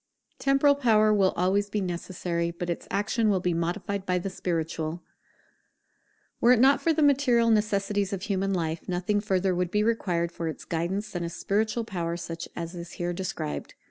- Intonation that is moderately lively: Yes, average, 3.7 semitones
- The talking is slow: No, average, 180 wpm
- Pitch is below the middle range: No, high, 190 Hz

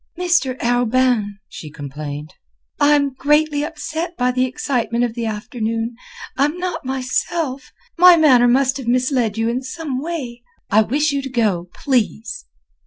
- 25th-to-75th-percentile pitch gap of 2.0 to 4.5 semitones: Yes, average, 4.0 semitones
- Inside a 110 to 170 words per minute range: Yes, average, 145 wpm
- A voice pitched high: Yes, very high, 255 Hz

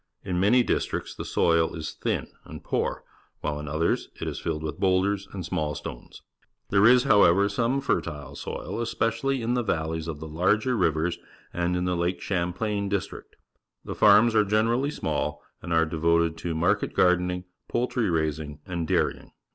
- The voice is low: Yes, very low, 90 Hz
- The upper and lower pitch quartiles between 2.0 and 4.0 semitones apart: No, average, 4.6 semitones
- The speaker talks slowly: No, average, 170 wpm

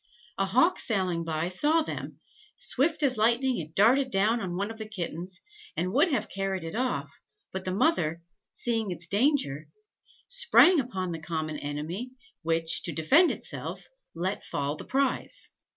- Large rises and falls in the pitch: Yes, wide, 7.4 semitones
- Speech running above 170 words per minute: No, average, 160 wpm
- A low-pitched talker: No, high, 195 Hz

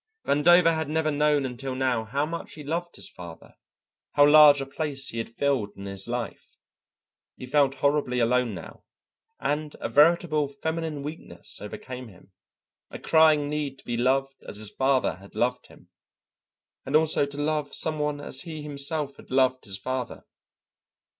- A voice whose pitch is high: No, medium, 140 Hz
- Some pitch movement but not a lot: Yes, average, 3.2 semitones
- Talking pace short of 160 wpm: No, average, 165 wpm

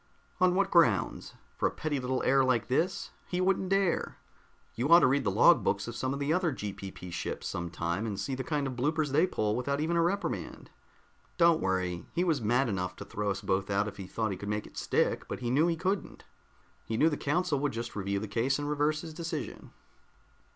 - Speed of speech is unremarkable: No, fast, 230 wpm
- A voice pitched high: No, low, 135 Hz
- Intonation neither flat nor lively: No, wide, 7.7 semitones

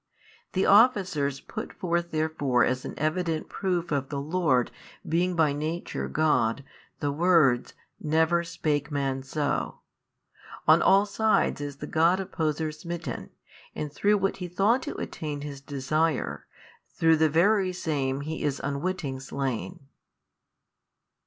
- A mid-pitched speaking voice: Yes, medium, 155 Hz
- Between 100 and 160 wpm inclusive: Yes, slow, 135 wpm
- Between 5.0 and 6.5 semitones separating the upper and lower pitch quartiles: No, average, 3.6 semitones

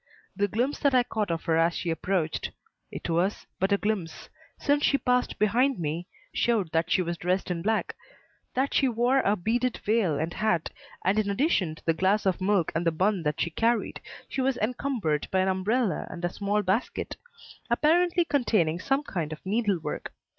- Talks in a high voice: Yes, high, 200 Hz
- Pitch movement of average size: No, wide, 5.9 semitones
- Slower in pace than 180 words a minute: No, average, 190 wpm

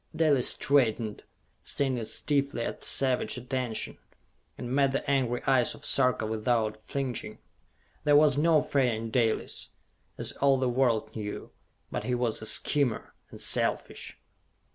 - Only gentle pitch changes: No, average, 3.3 semitones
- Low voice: Yes, low, 125 Hz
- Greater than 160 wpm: No, average, 140 wpm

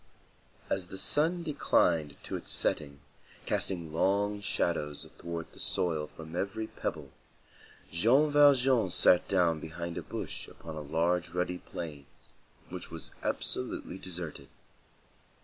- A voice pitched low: Yes, very low, 90 Hz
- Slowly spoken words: Yes, slow, 125 wpm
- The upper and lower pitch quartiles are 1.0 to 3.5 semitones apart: No, average, 4.1 semitones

